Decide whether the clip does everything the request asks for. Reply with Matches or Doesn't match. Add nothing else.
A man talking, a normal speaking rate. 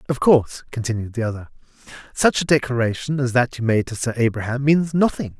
Matches